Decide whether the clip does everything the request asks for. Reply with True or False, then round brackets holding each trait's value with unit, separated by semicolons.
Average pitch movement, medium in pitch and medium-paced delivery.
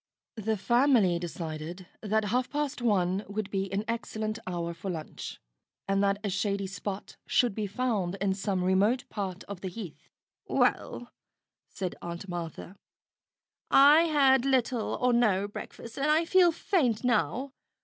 False (4.6 semitones; 205 Hz; 150 wpm)